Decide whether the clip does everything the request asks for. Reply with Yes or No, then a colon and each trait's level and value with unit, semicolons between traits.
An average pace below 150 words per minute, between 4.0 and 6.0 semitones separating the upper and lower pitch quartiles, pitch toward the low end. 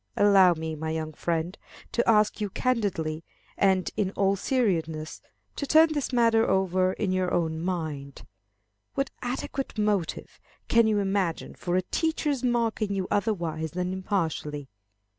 No: average, 140 wpm; average, 5.3 semitones; high, 190 Hz